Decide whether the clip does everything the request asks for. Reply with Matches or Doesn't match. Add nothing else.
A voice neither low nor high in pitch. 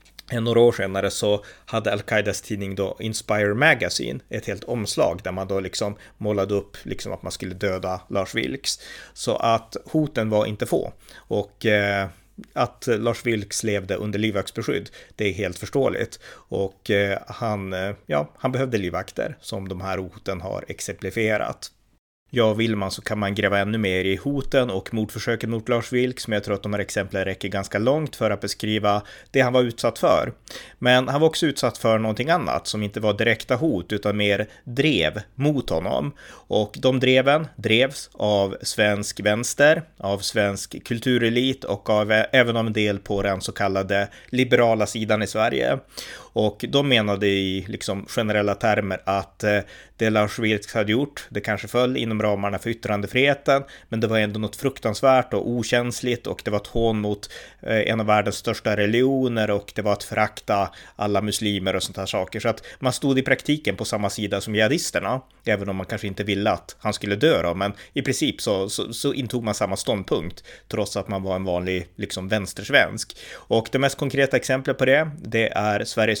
Doesn't match